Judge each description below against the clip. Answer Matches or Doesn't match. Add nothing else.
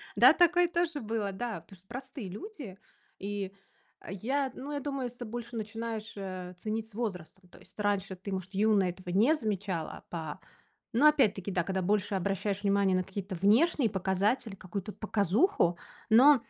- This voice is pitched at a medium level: Doesn't match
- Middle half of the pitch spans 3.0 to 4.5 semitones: Matches